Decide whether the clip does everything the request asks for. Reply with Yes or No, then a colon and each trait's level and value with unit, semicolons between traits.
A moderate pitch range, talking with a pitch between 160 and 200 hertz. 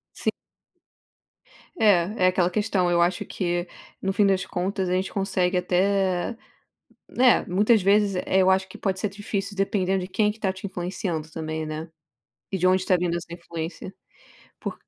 No: narrow, 1.9 semitones; medium, 185 Hz